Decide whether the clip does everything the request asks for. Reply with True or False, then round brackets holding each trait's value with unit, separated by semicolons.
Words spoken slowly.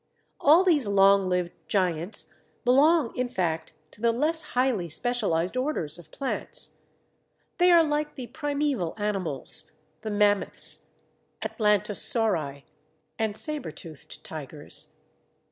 True (110 wpm)